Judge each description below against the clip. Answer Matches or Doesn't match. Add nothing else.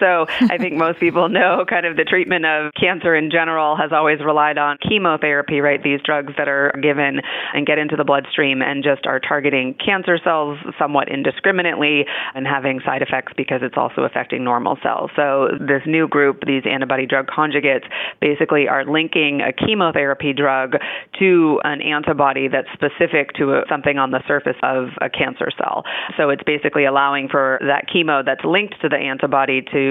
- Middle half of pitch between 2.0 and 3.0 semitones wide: Matches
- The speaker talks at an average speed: Matches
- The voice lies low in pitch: Doesn't match